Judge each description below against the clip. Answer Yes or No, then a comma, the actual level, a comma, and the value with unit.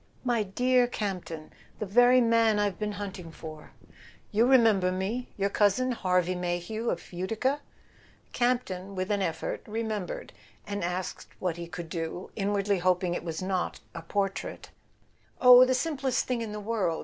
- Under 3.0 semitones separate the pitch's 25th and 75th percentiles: No, average, 4.2 semitones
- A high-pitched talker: Yes, high, 200 Hz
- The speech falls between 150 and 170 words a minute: Yes, average, 160 wpm